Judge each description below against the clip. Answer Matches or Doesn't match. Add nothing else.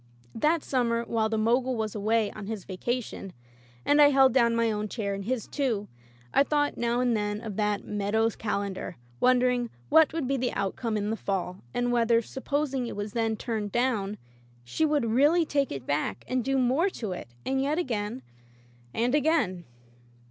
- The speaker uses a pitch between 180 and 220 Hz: Doesn't match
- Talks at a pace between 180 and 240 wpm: Matches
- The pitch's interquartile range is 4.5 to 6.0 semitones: Doesn't match